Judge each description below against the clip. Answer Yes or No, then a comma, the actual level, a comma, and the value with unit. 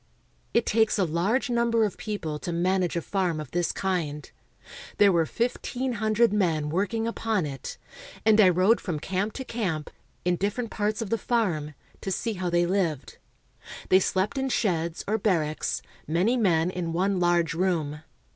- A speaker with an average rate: Yes, average, 170 wpm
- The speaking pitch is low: No, medium, 185 Hz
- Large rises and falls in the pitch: No, average, 4.6 semitones